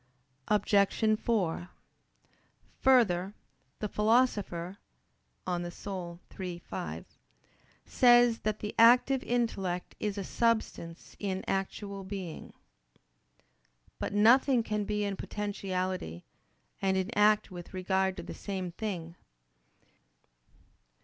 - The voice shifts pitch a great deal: No, average, 2.9 semitones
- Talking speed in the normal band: No, slow, 100 wpm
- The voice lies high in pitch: Yes, high, 200 Hz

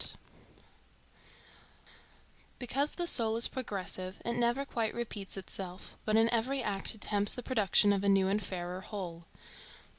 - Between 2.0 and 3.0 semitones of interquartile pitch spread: No, average, 3.7 semitones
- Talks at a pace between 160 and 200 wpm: No, average, 145 wpm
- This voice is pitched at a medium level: No, high, 210 Hz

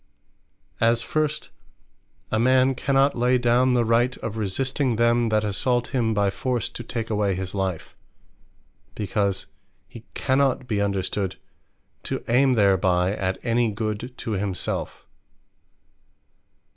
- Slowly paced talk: Yes, slow, 125 wpm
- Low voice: Yes, low, 115 Hz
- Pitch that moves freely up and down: No, average, 3.7 semitones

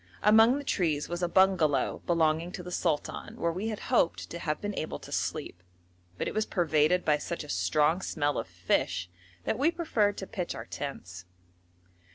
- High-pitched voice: No, medium, 170 Hz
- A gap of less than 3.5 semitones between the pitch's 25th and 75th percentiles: No, average, 4.9 semitones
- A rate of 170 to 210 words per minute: Yes, average, 190 wpm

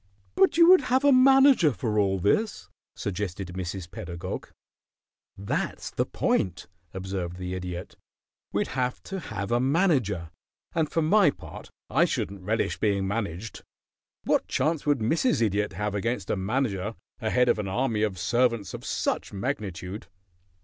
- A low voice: Yes, low, 105 Hz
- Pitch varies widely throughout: Yes, wide, 6.5 semitones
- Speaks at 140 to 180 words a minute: Yes, average, 150 wpm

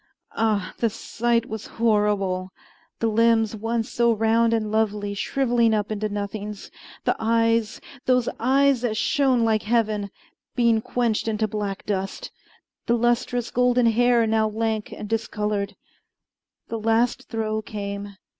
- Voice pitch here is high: Yes, high, 225 Hz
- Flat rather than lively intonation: Yes, narrow, 1.8 semitones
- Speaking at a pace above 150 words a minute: No, slow, 135 wpm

